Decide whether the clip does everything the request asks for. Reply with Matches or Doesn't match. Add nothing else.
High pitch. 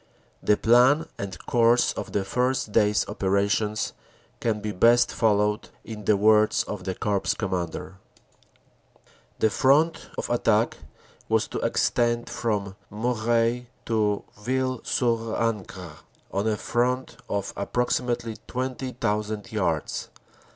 Doesn't match